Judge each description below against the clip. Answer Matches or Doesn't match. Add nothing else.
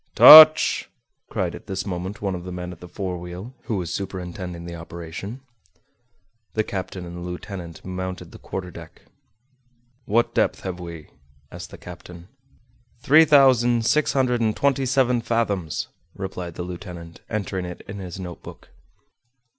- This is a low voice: Matches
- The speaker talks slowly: Doesn't match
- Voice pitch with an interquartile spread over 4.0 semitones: Matches